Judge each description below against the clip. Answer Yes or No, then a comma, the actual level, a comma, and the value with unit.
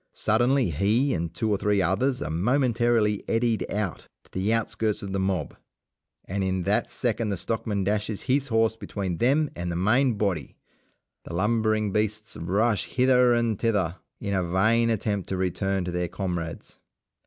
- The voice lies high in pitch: No, low, 105 Hz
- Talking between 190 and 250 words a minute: No, average, 165 wpm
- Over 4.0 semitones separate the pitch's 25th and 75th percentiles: No, average, 3.6 semitones